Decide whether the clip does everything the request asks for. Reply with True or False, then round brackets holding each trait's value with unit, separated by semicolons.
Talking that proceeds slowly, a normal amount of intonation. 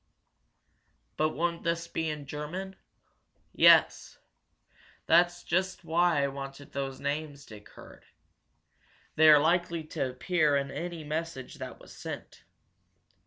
True (120 wpm; 3.3 semitones)